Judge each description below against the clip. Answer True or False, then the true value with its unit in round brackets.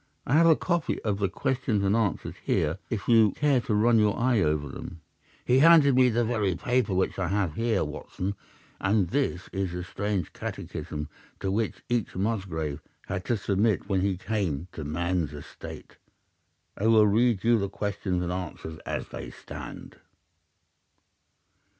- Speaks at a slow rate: False (165 wpm)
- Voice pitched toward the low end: True (100 Hz)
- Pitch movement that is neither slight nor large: True (4.2 semitones)